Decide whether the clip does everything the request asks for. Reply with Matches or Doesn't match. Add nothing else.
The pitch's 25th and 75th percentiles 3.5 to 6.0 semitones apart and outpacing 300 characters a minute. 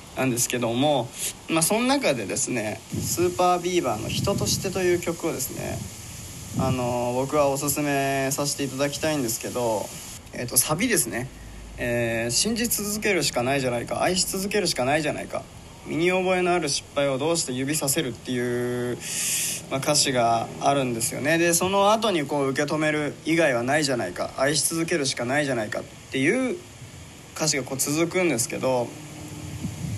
Matches